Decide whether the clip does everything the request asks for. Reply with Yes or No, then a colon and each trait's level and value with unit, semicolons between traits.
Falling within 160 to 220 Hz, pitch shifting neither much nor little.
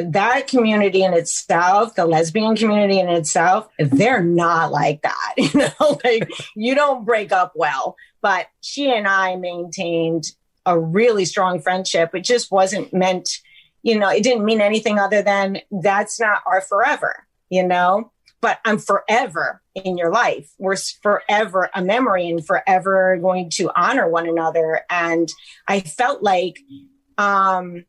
Yes: high, 190 Hz; average, 3.8 semitones